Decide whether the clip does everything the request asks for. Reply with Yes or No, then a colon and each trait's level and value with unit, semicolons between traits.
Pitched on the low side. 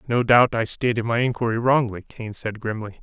Yes: low, 115 Hz